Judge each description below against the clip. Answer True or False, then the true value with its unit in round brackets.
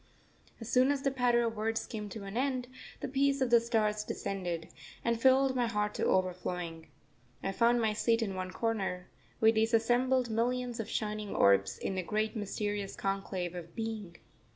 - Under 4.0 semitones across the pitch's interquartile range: True (3.6 semitones)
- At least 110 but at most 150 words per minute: False (180 wpm)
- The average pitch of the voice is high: True (220 Hz)